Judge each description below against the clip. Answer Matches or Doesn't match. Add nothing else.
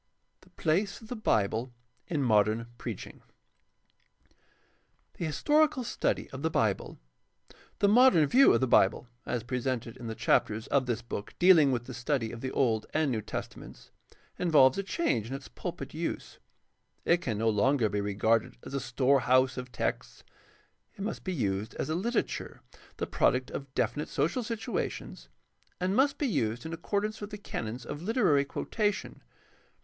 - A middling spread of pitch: Doesn't match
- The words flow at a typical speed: Matches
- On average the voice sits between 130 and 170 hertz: Matches